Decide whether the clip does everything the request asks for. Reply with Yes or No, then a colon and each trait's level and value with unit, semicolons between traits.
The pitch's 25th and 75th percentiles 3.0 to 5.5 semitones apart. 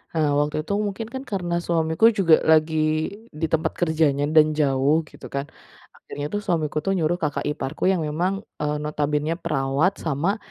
No: narrow, 2.6 semitones